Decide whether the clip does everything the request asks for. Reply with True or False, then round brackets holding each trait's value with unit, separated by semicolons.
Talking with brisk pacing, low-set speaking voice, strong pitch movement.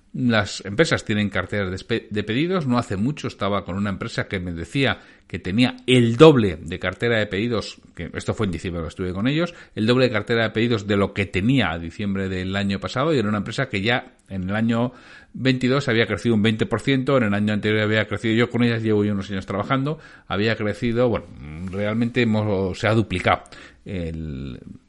False (205 wpm; 110 Hz; 3.7 semitones)